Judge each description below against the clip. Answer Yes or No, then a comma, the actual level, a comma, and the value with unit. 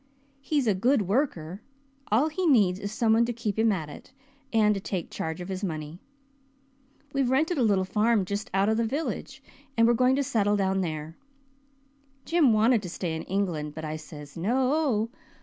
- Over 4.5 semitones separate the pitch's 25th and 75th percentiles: Yes, average, 5.1 semitones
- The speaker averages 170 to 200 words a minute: Yes, average, 190 wpm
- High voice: Yes, high, 210 Hz